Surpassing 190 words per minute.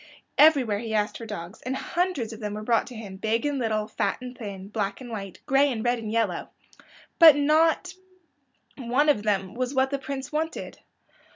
Yes: average, 200 wpm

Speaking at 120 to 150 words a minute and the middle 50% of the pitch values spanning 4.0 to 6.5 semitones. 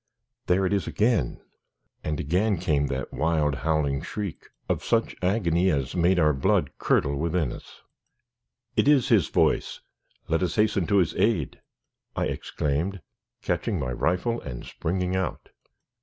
Yes: average, 145 wpm; average, 4.6 semitones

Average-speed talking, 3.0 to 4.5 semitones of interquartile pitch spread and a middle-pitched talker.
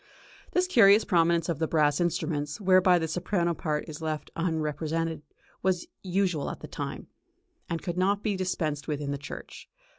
Yes: average, 170 wpm; average, 3.3 semitones; medium, 170 Hz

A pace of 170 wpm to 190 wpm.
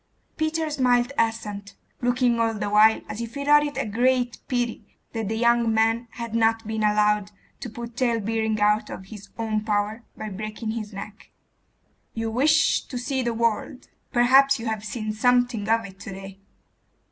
Yes: average, 175 wpm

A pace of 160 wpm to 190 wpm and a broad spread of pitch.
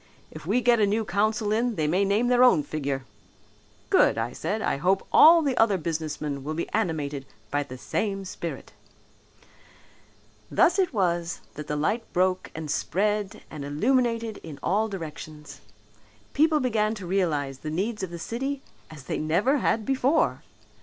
Yes: average, 165 wpm; wide, 6.7 semitones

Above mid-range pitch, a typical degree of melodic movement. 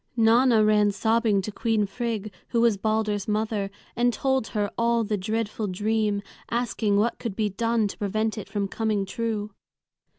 No: high, 215 Hz; narrow, 1.9 semitones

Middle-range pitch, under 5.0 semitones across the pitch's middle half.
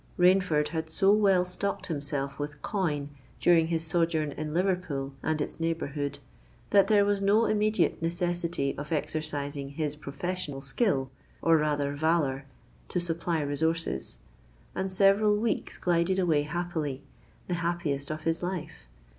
Yes: medium, 165 Hz; average, 3.7 semitones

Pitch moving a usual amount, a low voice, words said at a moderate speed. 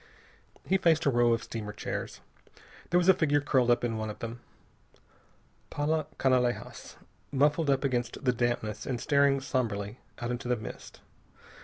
Yes: average, 3.4 semitones; low, 125 Hz; average, 160 wpm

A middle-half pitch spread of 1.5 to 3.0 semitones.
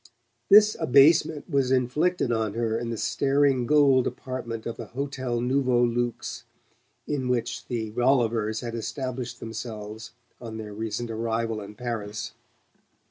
Yes: average, 2.7 semitones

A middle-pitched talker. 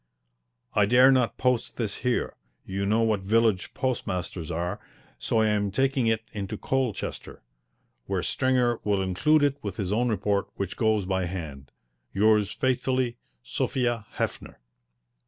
No: low, 110 Hz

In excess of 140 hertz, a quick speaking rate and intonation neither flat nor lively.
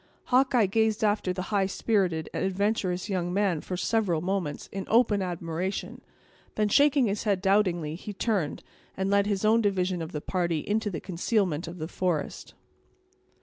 No: high, 190 Hz; average, 165 wpm; average, 3.0 semitones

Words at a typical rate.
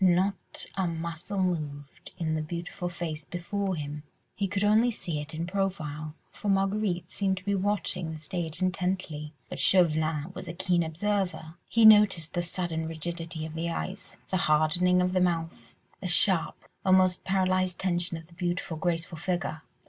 Yes: average, 165 wpm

